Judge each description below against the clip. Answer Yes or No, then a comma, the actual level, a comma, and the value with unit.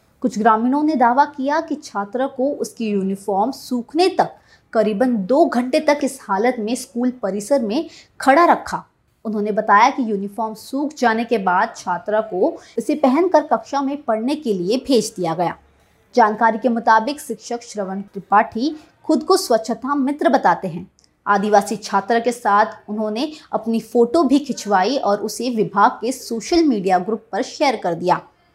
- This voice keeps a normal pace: Yes, average, 160 wpm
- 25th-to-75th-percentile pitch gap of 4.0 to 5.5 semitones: Yes, average, 4.6 semitones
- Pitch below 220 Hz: No, high, 230 Hz